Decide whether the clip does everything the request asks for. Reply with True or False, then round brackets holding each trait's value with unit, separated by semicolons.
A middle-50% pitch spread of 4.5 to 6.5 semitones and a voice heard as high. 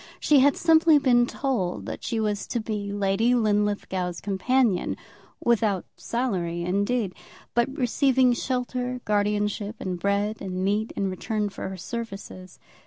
False (4.0 semitones; 210 Hz)